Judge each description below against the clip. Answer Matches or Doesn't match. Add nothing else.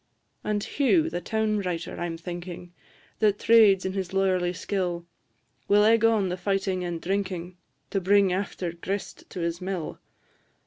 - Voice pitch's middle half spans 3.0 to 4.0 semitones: Doesn't match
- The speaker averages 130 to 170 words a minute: Matches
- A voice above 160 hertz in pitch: Matches